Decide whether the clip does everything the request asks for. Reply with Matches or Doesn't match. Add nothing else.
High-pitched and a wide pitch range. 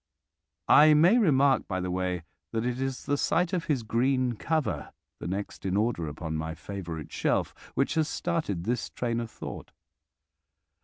Doesn't match